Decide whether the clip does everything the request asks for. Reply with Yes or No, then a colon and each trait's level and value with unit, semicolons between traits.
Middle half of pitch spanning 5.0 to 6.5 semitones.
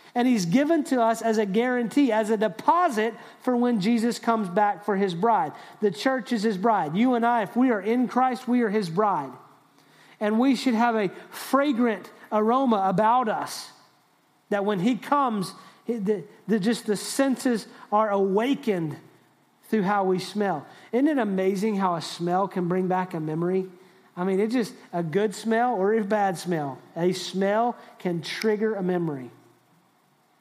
No: average, 3.7 semitones